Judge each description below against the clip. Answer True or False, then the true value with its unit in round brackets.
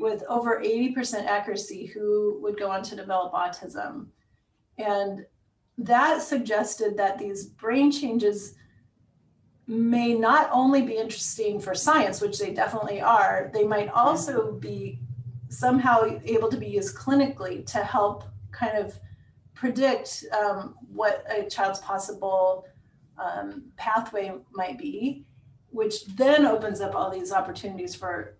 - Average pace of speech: False (130 wpm)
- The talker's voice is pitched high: True (210 Hz)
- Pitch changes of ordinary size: True (3.6 semitones)